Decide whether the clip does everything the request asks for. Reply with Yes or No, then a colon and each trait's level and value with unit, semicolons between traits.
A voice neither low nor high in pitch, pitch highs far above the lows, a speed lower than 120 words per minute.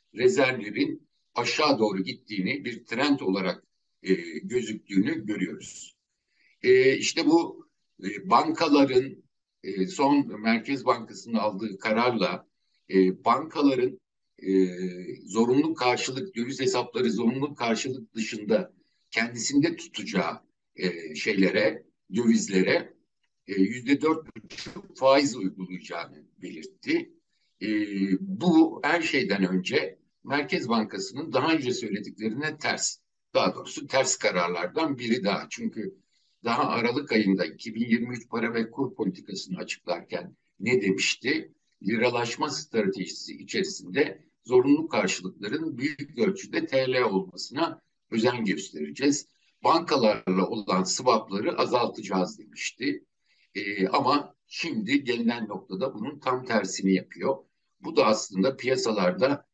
No: low, 125 Hz; wide, 6.4 semitones; average, 100 wpm